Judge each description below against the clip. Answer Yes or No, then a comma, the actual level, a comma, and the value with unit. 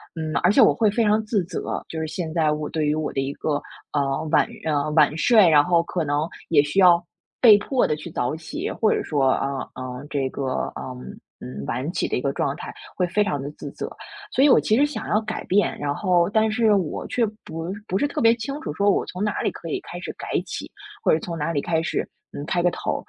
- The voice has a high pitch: No, medium, 165 Hz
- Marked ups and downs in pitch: Yes, wide, 6.0 semitones